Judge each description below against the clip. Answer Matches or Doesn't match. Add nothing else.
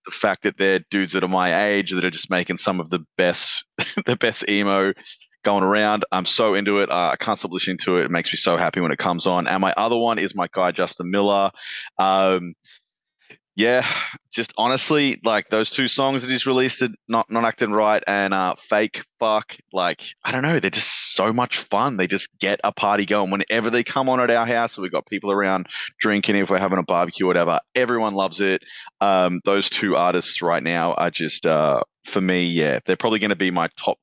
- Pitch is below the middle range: Matches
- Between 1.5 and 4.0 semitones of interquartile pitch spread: Matches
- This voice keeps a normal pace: Doesn't match